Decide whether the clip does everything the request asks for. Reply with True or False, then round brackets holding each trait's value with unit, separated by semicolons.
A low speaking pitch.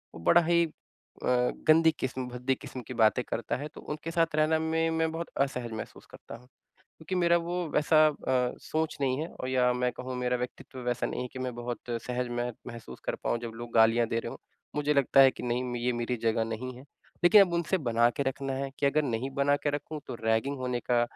True (130 Hz)